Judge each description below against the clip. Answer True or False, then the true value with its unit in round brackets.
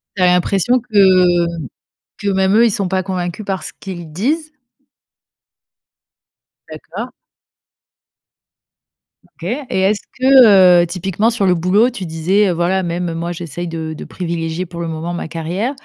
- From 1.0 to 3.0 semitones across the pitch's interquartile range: True (2.7 semitones)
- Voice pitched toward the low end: False (185 Hz)